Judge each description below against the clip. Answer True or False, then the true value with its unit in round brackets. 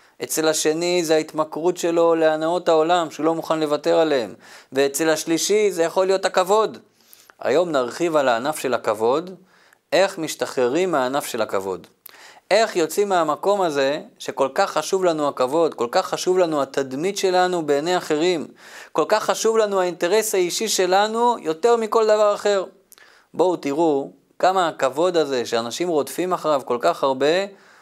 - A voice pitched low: False (170 Hz)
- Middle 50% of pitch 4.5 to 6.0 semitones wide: False (3.7 semitones)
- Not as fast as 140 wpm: False (145 wpm)